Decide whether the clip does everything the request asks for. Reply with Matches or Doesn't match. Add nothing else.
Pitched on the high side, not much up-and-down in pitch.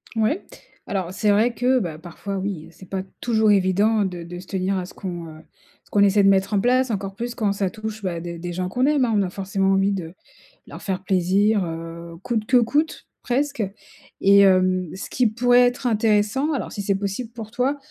Doesn't match